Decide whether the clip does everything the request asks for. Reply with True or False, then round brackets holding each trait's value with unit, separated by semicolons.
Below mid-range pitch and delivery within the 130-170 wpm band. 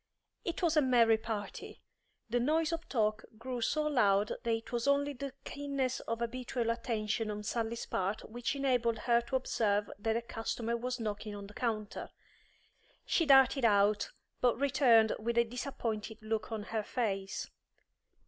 False (235 Hz; 160 wpm)